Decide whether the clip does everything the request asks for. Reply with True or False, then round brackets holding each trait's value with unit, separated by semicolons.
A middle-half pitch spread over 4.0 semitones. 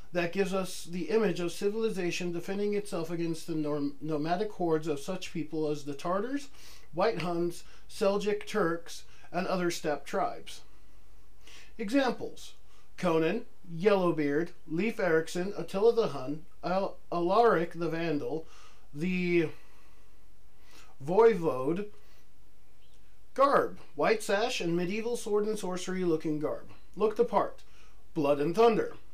True (4.5 semitones)